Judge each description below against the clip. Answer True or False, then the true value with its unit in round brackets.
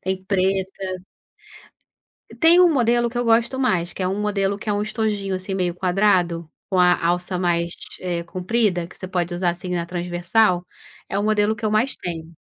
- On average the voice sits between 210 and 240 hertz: False (190 Hz)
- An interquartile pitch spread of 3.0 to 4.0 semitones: True (3.3 semitones)